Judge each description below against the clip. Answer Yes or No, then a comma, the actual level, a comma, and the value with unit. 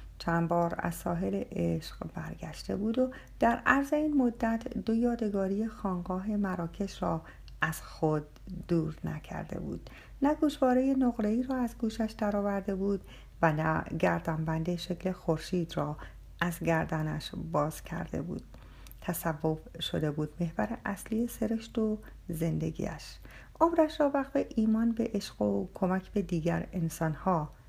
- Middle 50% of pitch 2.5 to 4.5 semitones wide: No, wide, 5.6 semitones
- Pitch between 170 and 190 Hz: Yes, medium, 185 Hz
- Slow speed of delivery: No, average, 130 wpm